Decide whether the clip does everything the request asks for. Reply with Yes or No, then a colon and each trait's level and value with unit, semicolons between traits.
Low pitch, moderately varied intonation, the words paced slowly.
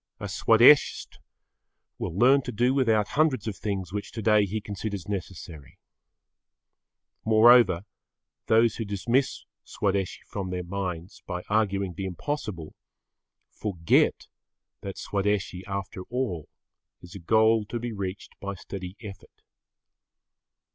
Yes: low, 100 Hz; average, 3.1 semitones; slow, 120 wpm